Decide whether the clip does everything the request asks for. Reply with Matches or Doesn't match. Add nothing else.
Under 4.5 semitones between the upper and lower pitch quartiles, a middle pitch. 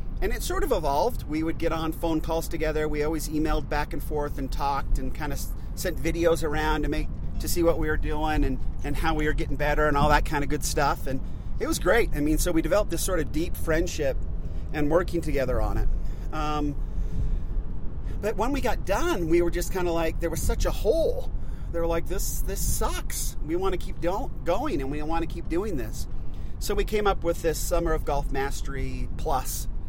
Matches